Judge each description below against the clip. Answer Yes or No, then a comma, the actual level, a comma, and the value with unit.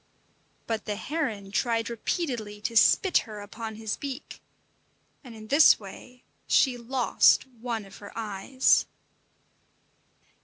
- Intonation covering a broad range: No, average, 3.3 semitones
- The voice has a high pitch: Yes, high, 230 Hz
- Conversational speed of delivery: No, slow, 120 wpm